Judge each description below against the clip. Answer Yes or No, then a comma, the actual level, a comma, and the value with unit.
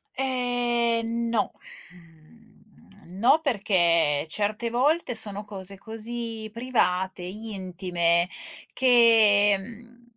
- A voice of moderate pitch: No, high, 215 Hz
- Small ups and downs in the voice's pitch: No, average, 4.0 semitones